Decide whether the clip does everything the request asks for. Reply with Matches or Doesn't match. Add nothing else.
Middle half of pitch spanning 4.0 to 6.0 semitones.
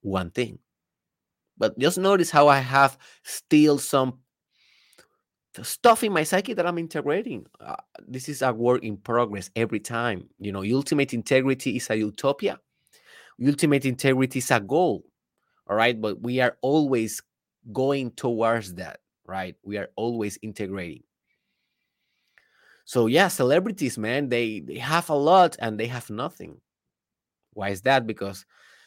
Matches